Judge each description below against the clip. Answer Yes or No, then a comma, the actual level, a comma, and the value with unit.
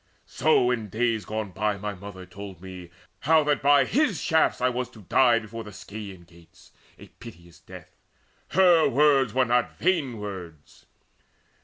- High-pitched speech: No, low, 110 Hz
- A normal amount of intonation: No, wide, 5.9 semitones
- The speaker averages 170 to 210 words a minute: No, average, 160 wpm